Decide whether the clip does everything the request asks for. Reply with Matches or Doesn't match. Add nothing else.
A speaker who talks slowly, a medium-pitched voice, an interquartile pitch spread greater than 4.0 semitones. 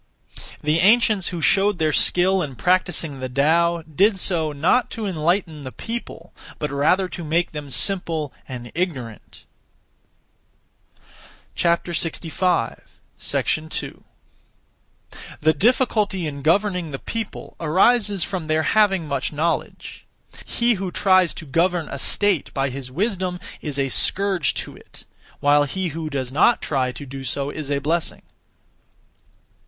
Matches